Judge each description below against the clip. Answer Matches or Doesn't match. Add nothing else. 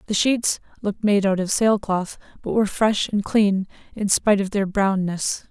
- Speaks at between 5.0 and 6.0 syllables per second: Doesn't match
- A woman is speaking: Matches